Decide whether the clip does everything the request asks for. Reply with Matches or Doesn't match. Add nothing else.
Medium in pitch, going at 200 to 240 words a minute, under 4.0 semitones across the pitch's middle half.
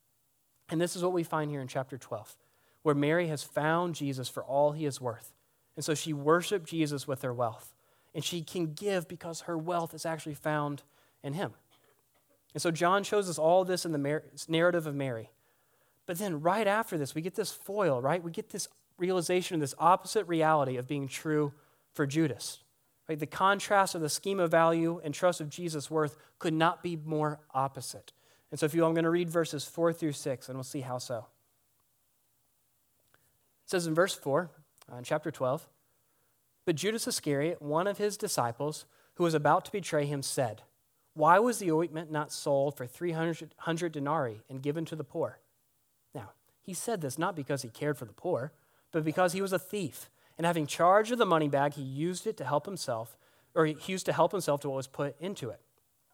Matches